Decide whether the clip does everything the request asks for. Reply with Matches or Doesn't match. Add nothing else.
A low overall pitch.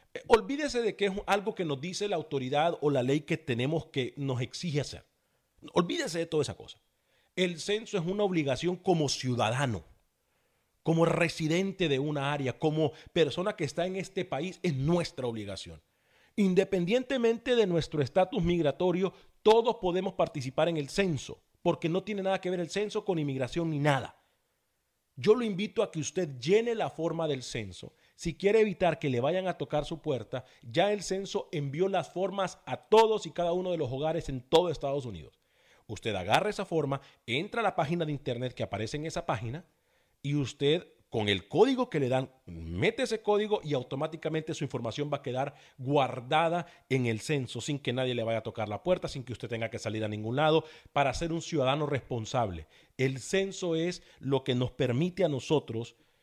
Doesn't match